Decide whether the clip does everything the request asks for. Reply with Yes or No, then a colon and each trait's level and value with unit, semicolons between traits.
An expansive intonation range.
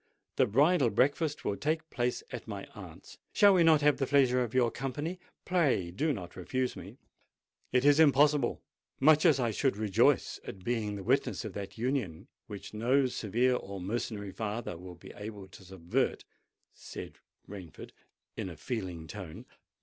Yes: wide, 6.1 semitones